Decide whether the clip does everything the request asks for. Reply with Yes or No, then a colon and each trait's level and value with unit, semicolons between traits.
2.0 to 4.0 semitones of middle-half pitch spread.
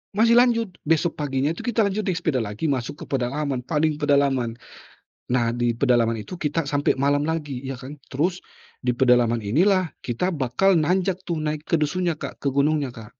No: average, 5.1 semitones